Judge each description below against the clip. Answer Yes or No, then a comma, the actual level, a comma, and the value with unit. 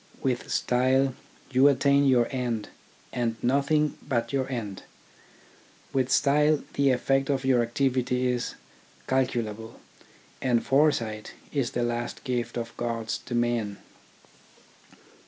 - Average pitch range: No, narrow, 2.3 semitones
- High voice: No, low, 125 Hz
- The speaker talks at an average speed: No, slow, 120 wpm